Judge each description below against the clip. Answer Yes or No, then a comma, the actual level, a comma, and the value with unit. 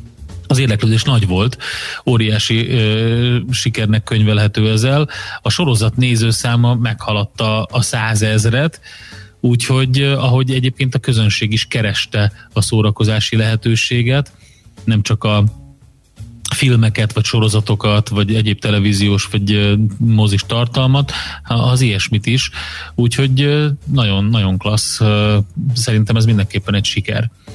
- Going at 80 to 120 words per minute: Yes, slow, 105 wpm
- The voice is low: Yes, low, 110 Hz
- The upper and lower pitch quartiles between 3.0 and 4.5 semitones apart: No, narrow, 2.6 semitones